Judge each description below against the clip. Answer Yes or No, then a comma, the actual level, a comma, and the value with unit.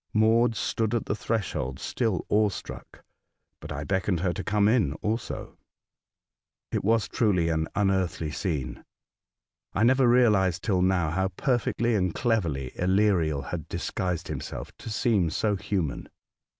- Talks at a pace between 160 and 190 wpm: No, average, 140 wpm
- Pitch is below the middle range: Yes, very low, 95 Hz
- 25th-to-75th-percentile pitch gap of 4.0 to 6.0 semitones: Yes, average, 4.7 semitones